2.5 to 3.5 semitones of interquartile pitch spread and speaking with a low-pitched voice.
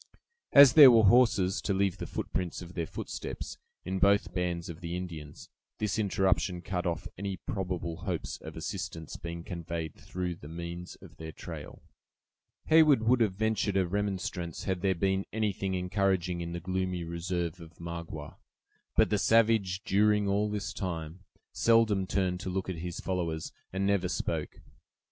Yes: average, 2.8 semitones; very low, 95 Hz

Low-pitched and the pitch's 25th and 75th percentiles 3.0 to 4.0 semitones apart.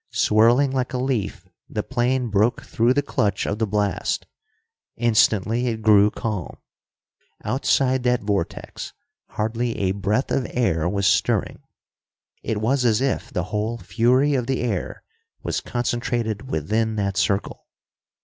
Yes: low, 115 Hz; average, 3.3 semitones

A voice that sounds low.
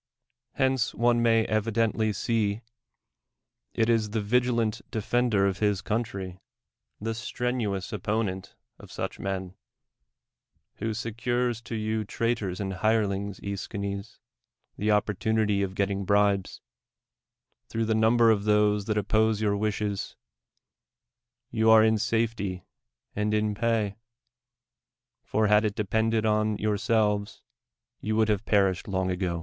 Yes: low, 105 Hz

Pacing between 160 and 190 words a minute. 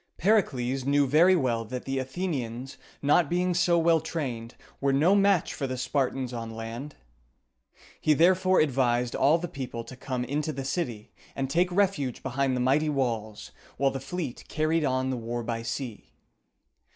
Yes: average, 165 wpm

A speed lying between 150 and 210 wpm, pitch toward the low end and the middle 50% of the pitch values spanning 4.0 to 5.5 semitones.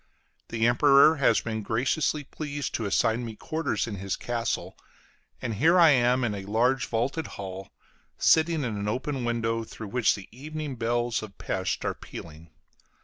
Yes: average, 165 wpm; low, 120 Hz; average, 4.3 semitones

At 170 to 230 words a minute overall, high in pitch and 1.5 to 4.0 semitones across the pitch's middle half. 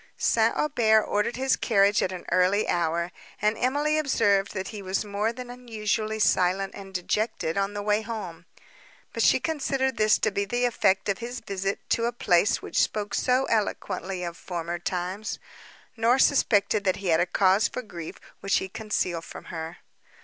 Yes: average, 180 wpm; high, 205 Hz; average, 3.5 semitones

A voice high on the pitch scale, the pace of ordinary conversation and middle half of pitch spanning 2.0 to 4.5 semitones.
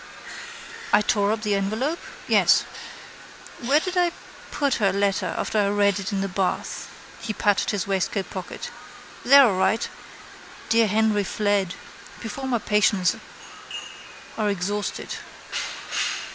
No: high, 205 Hz; slow, 125 wpm; narrow, 2.4 semitones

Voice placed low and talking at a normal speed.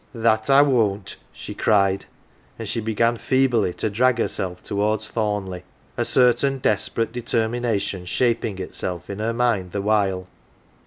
Yes: low, 110 Hz; average, 150 wpm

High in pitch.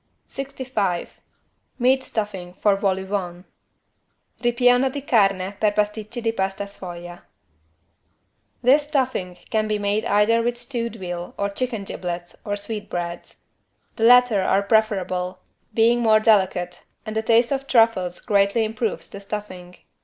Yes: high, 210 Hz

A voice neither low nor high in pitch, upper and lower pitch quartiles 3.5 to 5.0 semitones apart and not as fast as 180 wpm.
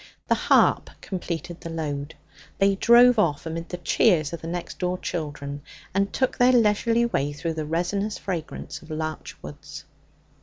Yes: medium, 170 Hz; average, 4.4 semitones; average, 160 wpm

